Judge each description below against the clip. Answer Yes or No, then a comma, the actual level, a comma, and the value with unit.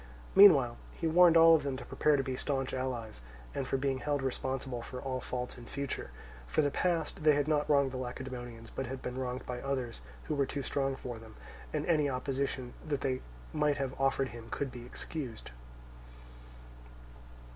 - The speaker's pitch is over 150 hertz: No, low, 135 Hz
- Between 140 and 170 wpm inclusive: No, average, 190 wpm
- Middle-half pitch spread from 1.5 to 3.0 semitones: Yes, narrow, 2.4 semitones